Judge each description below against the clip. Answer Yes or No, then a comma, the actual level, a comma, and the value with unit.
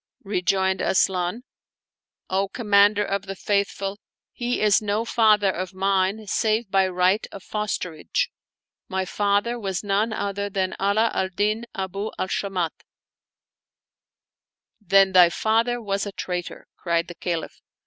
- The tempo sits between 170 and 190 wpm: No, average, 140 wpm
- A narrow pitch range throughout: Yes, narrow, 2.0 semitones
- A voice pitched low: No, high, 200 Hz